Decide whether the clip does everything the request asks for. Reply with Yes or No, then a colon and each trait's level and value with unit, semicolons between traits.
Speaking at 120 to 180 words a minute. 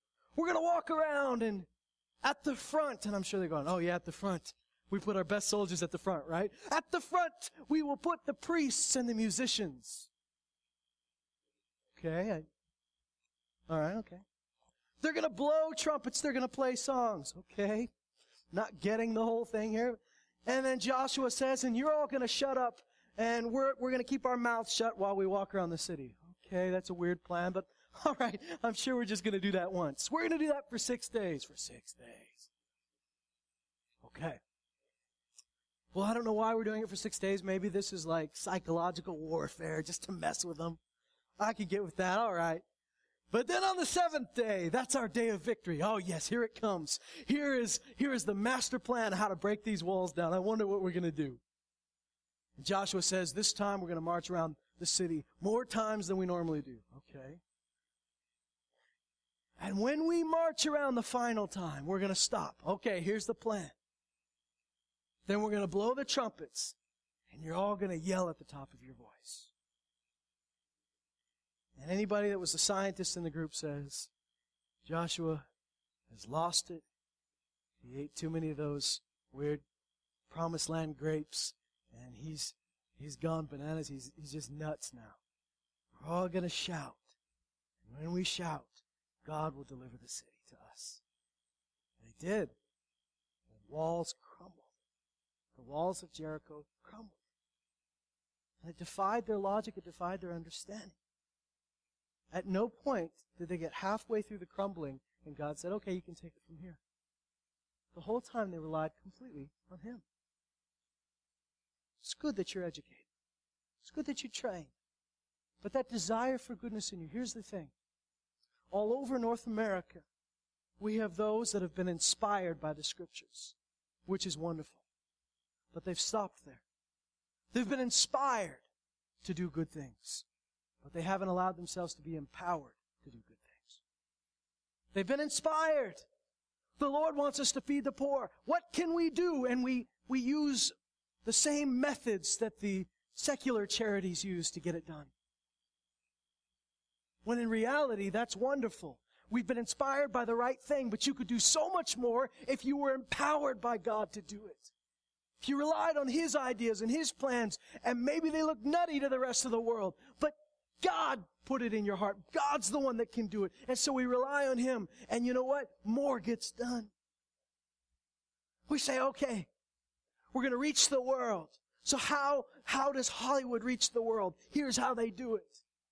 Yes: average, 175 wpm